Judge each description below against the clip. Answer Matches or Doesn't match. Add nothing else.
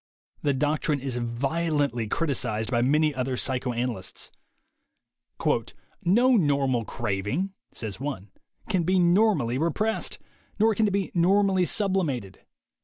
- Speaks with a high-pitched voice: Doesn't match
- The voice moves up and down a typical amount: Doesn't match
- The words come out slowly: Matches